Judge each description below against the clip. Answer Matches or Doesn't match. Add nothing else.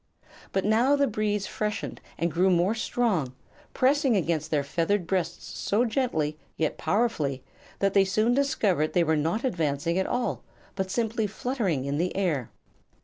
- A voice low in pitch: Doesn't match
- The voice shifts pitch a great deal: Matches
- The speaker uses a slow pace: Doesn't match